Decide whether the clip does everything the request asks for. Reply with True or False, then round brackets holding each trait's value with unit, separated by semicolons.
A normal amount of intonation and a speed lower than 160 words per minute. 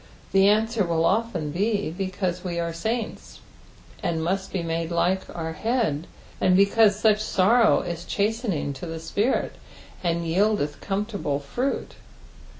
True (4.3 semitones; 140 wpm)